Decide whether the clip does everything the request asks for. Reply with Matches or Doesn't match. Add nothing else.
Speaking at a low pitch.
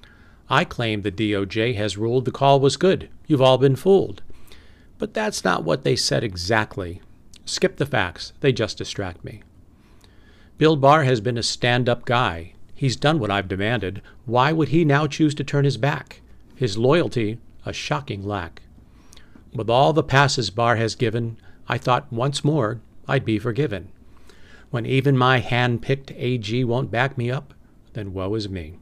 Matches